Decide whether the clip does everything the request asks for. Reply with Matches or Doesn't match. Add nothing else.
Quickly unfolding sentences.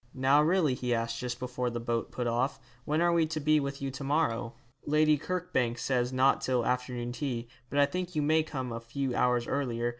Matches